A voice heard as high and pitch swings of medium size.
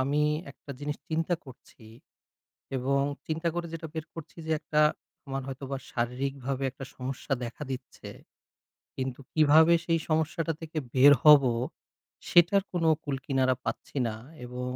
No: medium, 140 Hz; average, 3.4 semitones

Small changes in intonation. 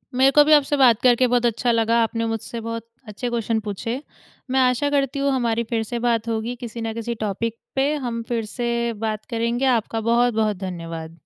Yes: narrow, 1.8 semitones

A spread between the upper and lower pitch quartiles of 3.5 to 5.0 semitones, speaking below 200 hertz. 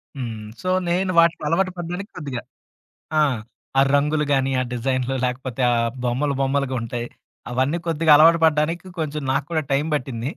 Yes: average, 4.0 semitones; medium, 140 Hz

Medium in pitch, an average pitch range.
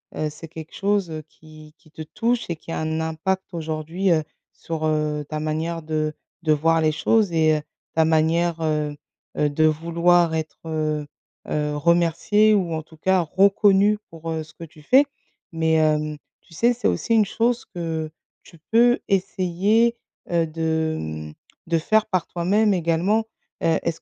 Yes: medium, 165 Hz; average, 3.1 semitones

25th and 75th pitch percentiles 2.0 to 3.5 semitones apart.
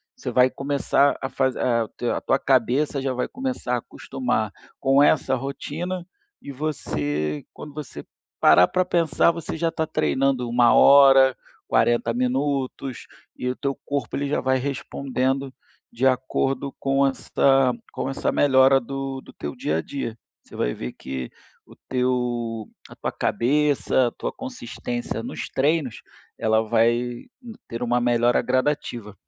Yes: narrow, 2.5 semitones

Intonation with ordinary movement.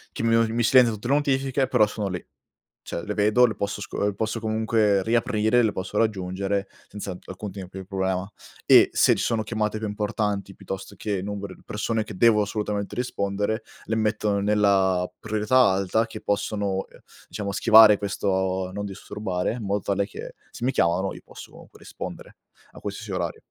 No: narrow, 2.1 semitones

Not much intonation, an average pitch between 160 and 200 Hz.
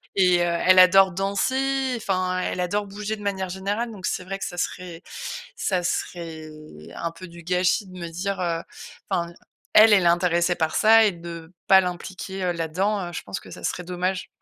Yes: narrow, 2.2 semitones; medium, 185 Hz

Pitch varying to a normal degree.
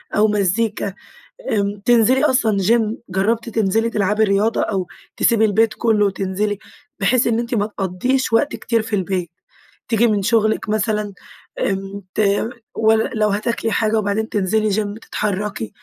No: narrow, 2.1 semitones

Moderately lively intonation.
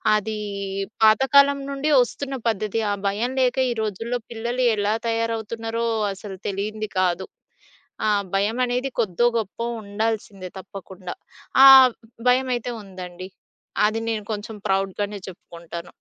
Yes: average, 3.5 semitones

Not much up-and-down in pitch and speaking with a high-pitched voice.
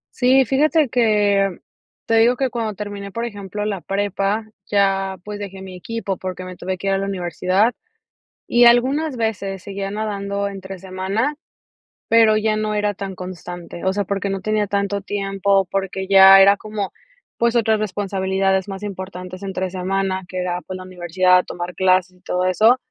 Yes: narrow, 2.1 semitones; high, 195 Hz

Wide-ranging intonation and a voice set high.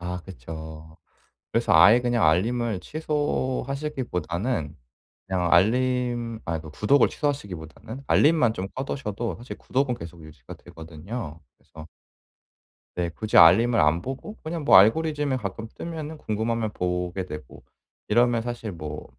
No: wide, 6.9 semitones; low, 110 Hz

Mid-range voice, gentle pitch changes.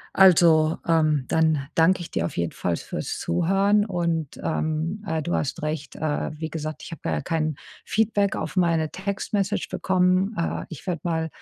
No: medium, 165 Hz; average, 3.2 semitones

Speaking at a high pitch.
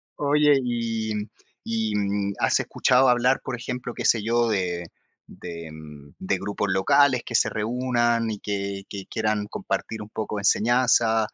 No: low, 110 Hz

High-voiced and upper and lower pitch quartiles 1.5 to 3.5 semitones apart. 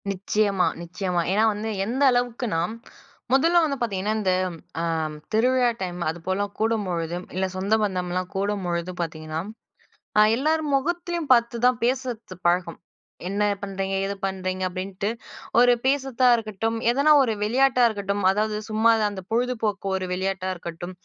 No: high, 205 Hz; average, 4.7 semitones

